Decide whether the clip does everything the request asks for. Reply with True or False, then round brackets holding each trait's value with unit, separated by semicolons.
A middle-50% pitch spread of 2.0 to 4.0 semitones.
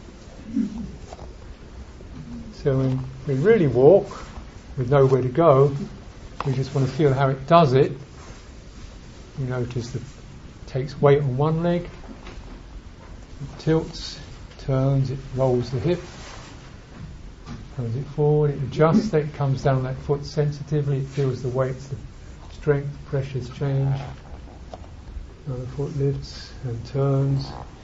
True (2.8 semitones)